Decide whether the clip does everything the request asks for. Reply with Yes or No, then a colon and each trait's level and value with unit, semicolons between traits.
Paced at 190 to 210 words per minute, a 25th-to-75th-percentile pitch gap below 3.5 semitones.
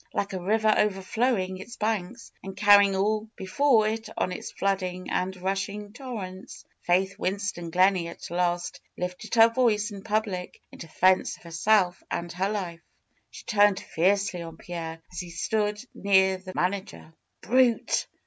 No: average, 160 wpm; average, 2.8 semitones